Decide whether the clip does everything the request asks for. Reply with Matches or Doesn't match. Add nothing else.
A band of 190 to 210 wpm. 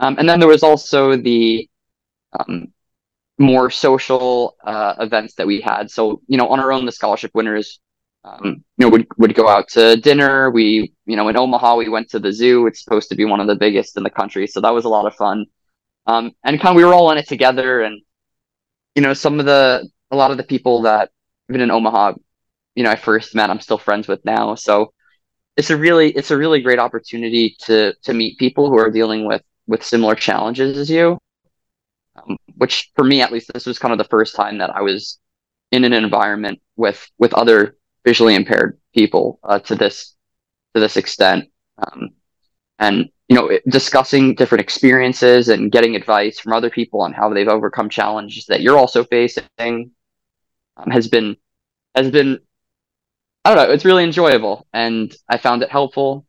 Matches